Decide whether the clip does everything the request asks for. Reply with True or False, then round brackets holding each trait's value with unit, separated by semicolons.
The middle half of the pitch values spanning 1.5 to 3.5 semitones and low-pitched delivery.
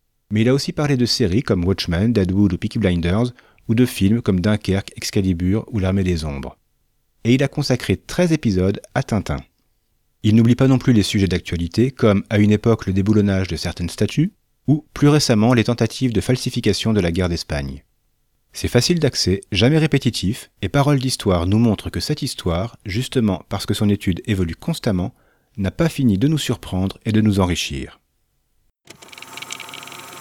False (5.1 semitones; 110 Hz)